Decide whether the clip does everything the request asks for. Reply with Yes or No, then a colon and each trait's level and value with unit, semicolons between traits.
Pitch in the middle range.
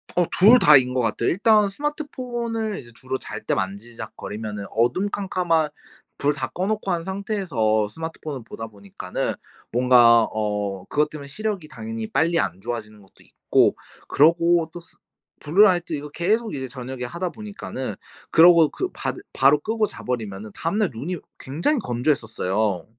Yes: medium, 150 Hz